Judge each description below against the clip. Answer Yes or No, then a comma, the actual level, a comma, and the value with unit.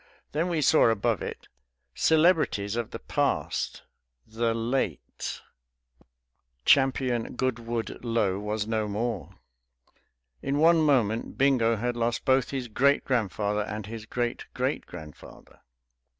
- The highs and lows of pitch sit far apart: No, average, 3.9 semitones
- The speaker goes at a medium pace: No, slow, 120 wpm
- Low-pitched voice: Yes, low, 115 Hz